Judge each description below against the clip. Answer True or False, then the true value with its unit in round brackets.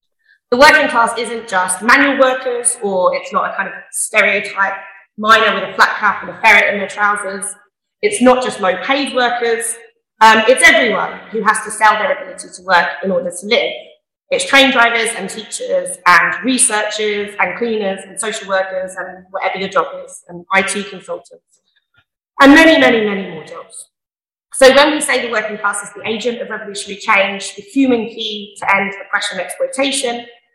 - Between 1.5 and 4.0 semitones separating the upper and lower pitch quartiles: False (4.6 semitones)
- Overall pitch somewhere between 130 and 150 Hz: False (220 Hz)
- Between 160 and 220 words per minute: True (185 wpm)